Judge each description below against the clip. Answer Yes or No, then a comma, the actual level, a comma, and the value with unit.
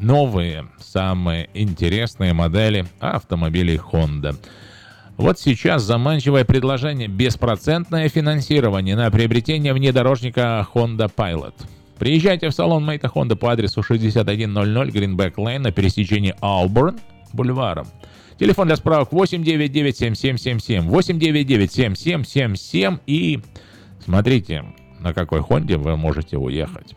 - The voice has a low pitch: Yes, low, 115 Hz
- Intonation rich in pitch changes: Yes, wide, 6.0 semitones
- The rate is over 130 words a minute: No, slow, 110 wpm